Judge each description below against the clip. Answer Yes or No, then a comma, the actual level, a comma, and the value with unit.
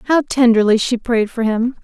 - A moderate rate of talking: Yes, average, 195 wpm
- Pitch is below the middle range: No, high, 235 Hz